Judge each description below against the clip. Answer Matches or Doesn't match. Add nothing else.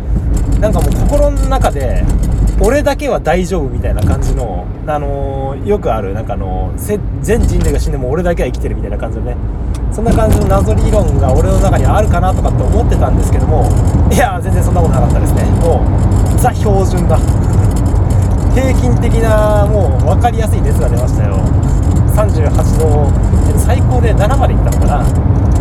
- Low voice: Matches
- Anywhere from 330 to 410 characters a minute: Matches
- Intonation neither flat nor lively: Doesn't match